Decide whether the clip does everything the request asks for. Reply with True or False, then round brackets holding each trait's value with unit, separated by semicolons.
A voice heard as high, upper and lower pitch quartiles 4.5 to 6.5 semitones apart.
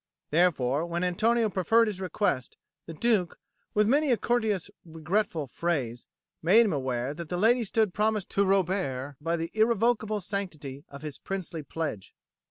False (180 Hz; 5.6 semitones)